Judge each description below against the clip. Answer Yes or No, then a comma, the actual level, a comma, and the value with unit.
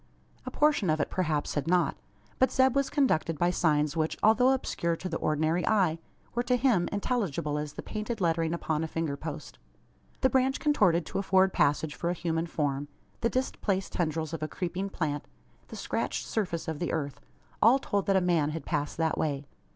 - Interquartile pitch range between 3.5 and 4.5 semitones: No, average, 5.0 semitones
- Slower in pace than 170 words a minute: No, average, 195 wpm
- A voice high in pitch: No, medium, 170 Hz